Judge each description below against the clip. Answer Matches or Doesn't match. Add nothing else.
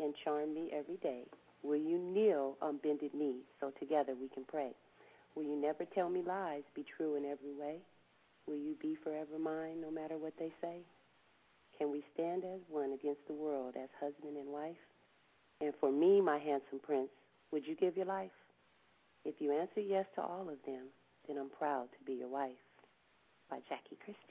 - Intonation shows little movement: Matches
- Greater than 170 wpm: Matches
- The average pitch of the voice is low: Doesn't match